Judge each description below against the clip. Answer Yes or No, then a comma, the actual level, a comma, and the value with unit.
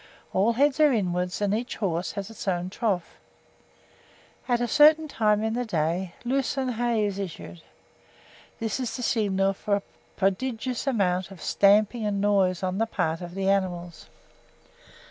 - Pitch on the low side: No, high, 205 Hz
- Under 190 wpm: Yes, average, 160 wpm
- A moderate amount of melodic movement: Yes, average, 4.1 semitones